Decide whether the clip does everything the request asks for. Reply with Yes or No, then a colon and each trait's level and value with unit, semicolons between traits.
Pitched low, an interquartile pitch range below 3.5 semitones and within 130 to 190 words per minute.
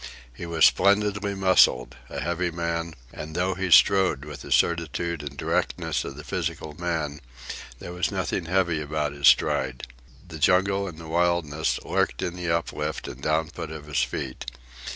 Yes: very low, 85 Hz; average, 2.9 semitones; average, 165 wpm